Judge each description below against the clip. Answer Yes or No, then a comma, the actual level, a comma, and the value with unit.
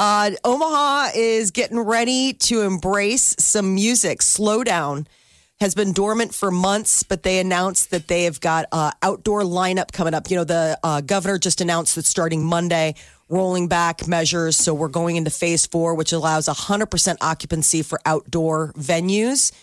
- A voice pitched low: No, medium, 180 Hz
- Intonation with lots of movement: No, average, 4.0 semitones